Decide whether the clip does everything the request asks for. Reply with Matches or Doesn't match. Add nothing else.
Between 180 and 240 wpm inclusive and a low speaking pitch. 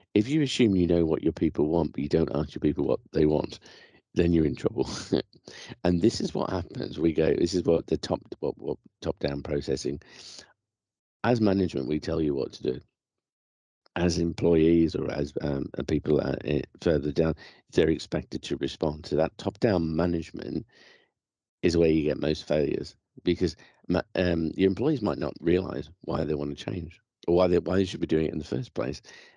Matches